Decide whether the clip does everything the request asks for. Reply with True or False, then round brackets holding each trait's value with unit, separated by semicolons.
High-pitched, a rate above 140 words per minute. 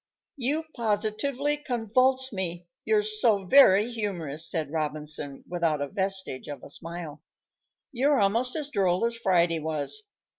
False (195 Hz; 135 wpm)